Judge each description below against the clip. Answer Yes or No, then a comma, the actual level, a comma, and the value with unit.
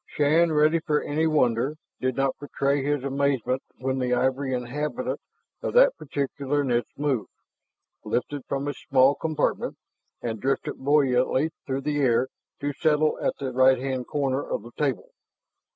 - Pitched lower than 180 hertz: Yes, medium, 140 Hz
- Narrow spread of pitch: Yes, narrow, 2.2 semitones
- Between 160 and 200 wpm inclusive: No, average, 150 wpm